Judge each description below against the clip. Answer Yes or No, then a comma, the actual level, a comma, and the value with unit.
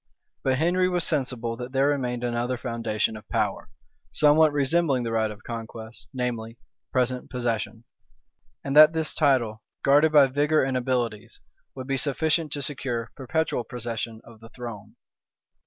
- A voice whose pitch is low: Yes, low, 125 Hz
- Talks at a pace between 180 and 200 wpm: No, average, 150 wpm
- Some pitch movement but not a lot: Yes, average, 3.8 semitones